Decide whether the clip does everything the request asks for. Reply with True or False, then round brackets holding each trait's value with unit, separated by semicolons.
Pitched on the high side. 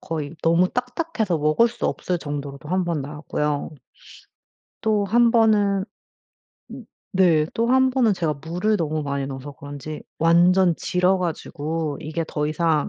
False (170 Hz)